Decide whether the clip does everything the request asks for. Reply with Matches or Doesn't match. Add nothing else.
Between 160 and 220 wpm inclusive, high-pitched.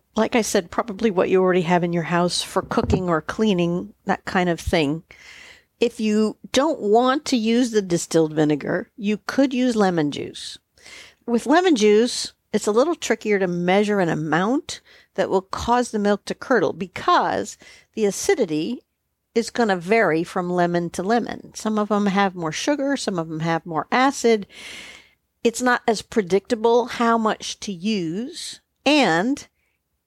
Matches